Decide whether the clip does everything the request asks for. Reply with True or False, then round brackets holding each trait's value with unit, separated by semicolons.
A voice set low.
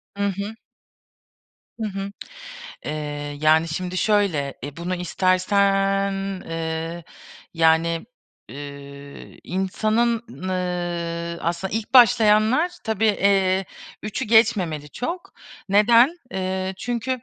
False (190 Hz)